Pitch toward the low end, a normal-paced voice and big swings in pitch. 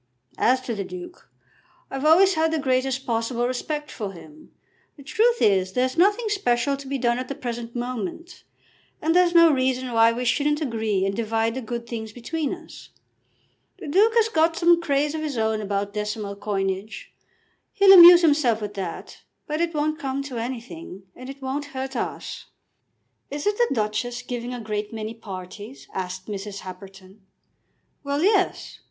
No: very high, 255 Hz; average, 170 wpm; wide, 6.1 semitones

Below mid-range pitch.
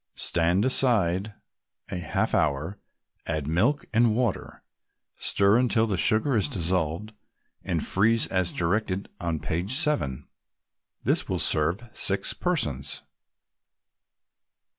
Yes: very low, 95 Hz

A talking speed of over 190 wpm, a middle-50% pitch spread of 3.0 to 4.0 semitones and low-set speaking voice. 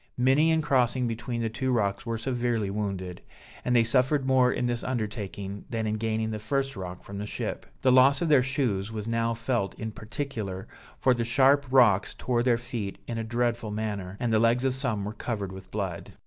Yes: fast, 205 wpm; average, 3.4 semitones; low, 115 Hz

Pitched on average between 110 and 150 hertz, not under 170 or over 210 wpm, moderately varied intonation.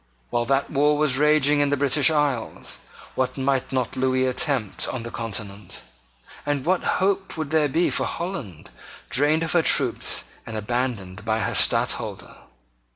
No: low, 135 Hz; average, 155 wpm; average, 4.0 semitones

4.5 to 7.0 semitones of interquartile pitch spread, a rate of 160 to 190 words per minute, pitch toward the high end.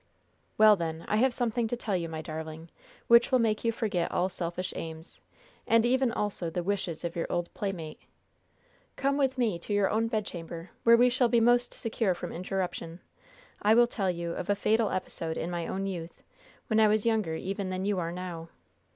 No: average, 5.0 semitones; average, 200 wpm; high, 195 Hz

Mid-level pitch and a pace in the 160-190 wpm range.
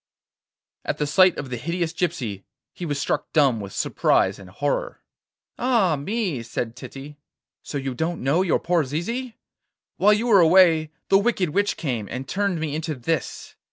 Yes: medium, 160 Hz; average, 170 wpm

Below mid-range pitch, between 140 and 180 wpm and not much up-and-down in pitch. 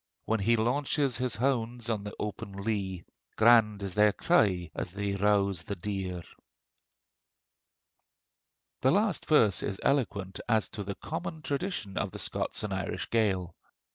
No: low, 105 Hz; average, 145 wpm; average, 3.9 semitones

